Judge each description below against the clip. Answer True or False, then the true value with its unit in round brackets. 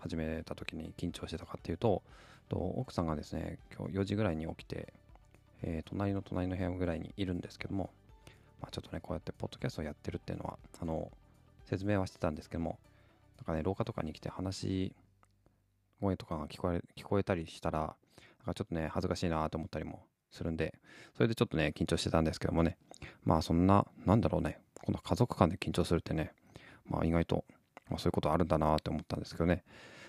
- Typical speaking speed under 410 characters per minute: False (460 characters per minute)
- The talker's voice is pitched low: True (90 Hz)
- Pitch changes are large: False (3.4 semitones)